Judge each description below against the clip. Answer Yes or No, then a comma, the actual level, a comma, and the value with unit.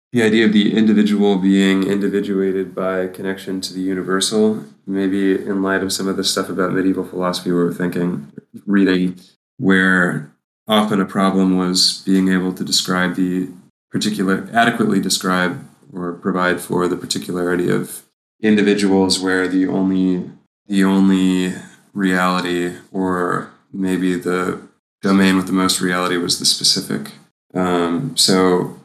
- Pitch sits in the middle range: No, very low, 95 Hz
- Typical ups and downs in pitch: No, narrow, 1.0 semitones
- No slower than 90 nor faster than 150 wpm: Yes, slow, 135 wpm